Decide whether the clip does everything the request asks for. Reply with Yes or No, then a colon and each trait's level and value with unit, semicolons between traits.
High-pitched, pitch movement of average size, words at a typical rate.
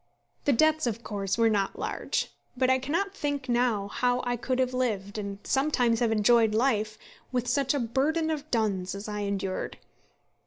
Yes: high, 240 Hz; average, 4.1 semitones; average, 180 wpm